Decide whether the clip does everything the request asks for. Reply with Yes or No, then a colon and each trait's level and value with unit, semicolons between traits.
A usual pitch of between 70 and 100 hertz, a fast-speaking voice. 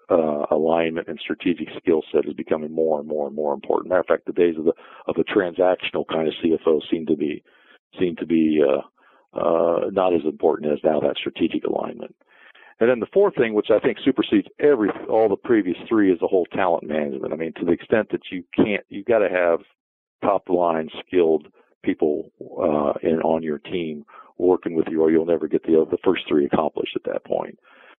Yes: very low, 85 Hz; fast, 210 wpm